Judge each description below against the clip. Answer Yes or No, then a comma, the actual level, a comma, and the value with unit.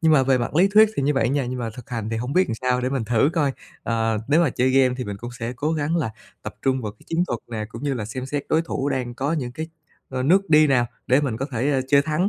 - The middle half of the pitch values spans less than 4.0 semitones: Yes, average, 3.6 semitones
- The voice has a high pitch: No, low, 130 Hz